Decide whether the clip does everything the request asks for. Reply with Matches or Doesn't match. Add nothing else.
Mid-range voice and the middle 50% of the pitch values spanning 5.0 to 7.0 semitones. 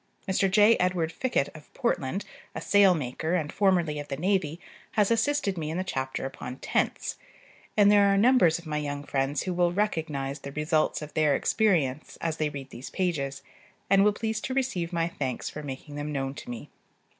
Matches